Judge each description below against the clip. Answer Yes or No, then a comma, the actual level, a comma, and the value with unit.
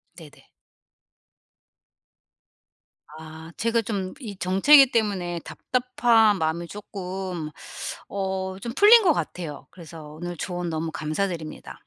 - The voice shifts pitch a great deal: No, average, 5.0 semitones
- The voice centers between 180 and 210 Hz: Yes, high, 190 Hz